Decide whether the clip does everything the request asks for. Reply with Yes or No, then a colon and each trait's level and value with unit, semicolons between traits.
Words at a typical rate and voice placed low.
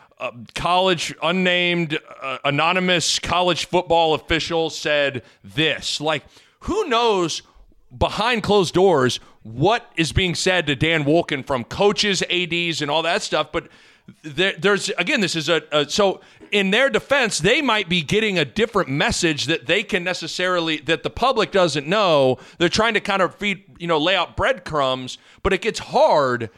No: average, 165 wpm; medium, 170 Hz